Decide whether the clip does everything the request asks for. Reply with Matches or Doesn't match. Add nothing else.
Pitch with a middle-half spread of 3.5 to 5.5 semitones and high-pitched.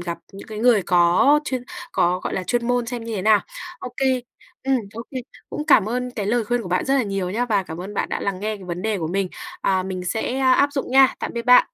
Matches